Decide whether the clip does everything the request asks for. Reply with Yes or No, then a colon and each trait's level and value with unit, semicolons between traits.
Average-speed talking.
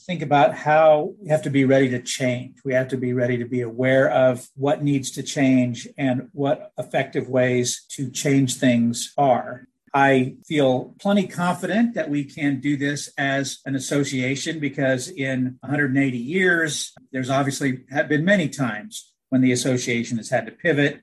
Yes: average, 170 wpm